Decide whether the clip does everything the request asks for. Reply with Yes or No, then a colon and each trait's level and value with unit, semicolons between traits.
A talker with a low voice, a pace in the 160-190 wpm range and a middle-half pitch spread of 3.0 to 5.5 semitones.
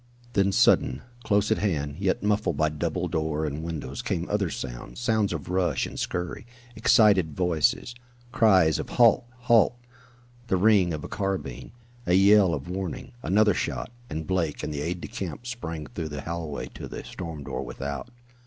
Yes: very low, 90 Hz; average, 170 wpm; average, 4.8 semitones